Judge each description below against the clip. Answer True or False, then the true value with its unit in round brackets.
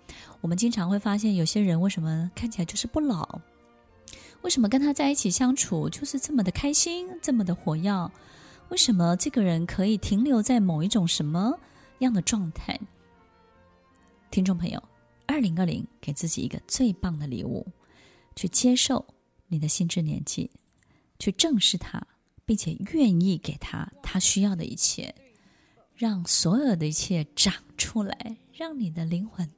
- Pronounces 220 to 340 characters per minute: True (240 characters per minute)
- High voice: True (195 Hz)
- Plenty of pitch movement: True (6.1 semitones)